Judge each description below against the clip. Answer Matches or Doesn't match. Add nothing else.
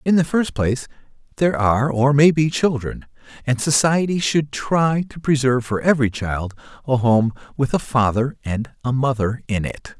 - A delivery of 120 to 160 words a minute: Doesn't match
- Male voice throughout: Matches